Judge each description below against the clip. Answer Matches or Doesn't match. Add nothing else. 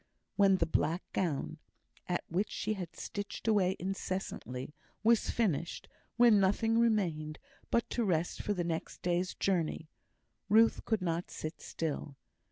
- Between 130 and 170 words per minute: Matches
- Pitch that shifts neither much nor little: Matches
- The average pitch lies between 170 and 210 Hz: Matches